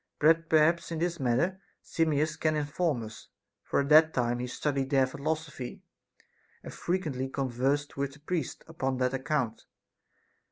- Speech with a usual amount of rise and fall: Yes, average, 3.3 semitones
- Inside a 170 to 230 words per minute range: No, average, 150 wpm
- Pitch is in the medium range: Yes, medium, 145 Hz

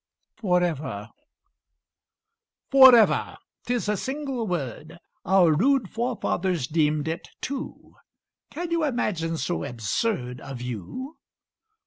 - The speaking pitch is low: No, medium, 180 Hz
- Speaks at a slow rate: Yes, slow, 95 wpm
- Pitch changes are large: Yes, wide, 8.8 semitones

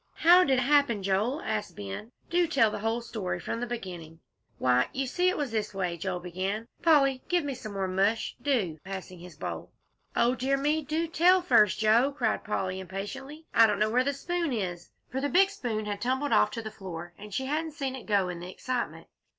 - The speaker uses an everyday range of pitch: No, wide, 6.6 semitones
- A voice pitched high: Yes, high, 225 Hz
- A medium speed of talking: No, fast, 215 wpm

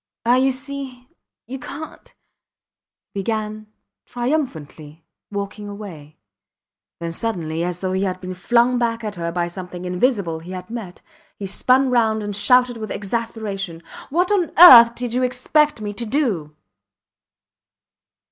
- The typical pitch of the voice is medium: No, high, 215 Hz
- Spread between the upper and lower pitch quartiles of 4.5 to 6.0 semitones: Yes, wide, 5.4 semitones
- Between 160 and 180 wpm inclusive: No, average, 140 wpm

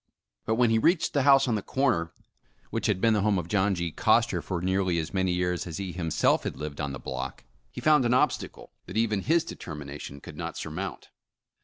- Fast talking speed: Yes, fast, 215 wpm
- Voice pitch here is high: No, very low, 95 Hz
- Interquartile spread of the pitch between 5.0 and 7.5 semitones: Yes, wide, 5.5 semitones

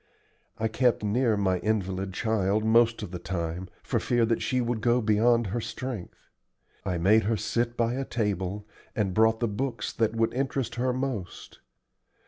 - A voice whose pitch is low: Yes, low, 110 Hz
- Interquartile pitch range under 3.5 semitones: Yes, average, 3.1 semitones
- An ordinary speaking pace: Yes, average, 170 wpm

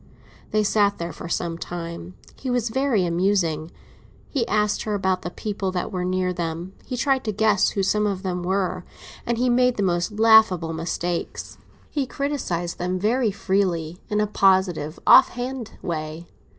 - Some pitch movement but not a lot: Yes, average, 3.9 semitones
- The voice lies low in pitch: No, high, 190 Hz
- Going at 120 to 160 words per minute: No, average, 170 wpm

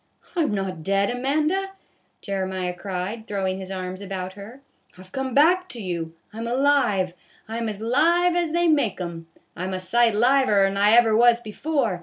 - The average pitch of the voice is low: No, high, 215 Hz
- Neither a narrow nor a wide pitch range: No, wide, 6.1 semitones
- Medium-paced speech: No, fast, 210 wpm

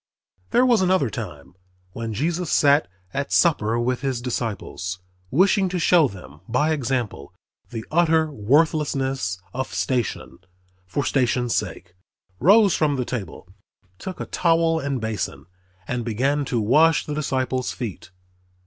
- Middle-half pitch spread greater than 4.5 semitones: Yes, wide, 5.4 semitones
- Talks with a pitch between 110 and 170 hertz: Yes, low, 135 Hz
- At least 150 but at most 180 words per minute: No, slow, 135 wpm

